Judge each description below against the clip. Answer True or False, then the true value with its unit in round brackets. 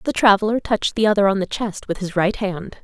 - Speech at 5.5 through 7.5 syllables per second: True (6.0 syllables/s)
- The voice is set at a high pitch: True (205 Hz)